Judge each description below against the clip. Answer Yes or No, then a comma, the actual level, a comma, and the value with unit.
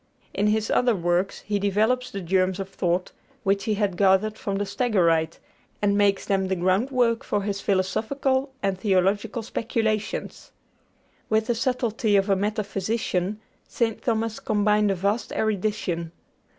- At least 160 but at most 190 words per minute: No, average, 145 wpm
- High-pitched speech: Yes, high, 205 Hz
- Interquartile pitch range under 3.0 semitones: Yes, narrow, 2.4 semitones